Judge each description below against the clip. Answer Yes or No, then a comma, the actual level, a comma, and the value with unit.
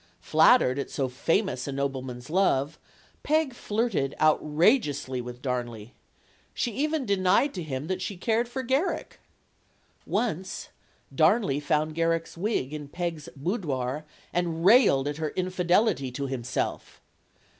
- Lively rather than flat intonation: Yes, wide, 6.9 semitones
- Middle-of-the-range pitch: Yes, medium, 160 Hz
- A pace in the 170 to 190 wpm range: No, slow, 135 wpm